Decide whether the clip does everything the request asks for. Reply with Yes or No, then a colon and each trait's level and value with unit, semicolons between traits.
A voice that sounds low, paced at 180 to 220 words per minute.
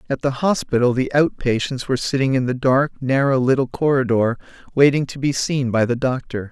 Yes: low, 130 Hz; average, 195 wpm